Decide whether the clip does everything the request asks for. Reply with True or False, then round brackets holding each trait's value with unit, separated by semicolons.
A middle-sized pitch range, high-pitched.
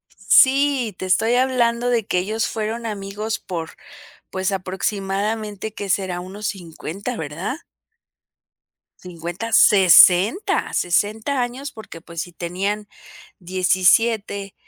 True (3.7 semitones; 200 Hz)